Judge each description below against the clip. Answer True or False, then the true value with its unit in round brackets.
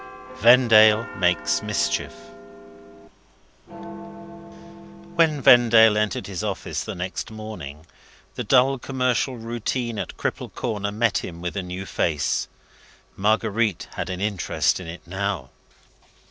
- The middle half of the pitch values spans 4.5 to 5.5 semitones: True (4.8 semitones)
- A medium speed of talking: False (115 wpm)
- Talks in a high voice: False (105 Hz)